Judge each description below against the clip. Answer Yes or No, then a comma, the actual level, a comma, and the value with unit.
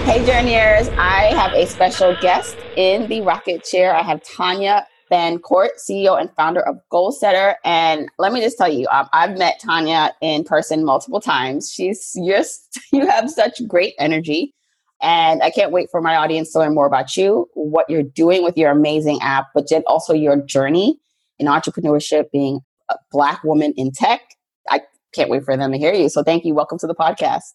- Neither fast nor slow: Yes, average, 190 wpm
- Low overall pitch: No, medium, 165 Hz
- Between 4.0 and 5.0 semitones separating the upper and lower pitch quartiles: Yes, average, 4.5 semitones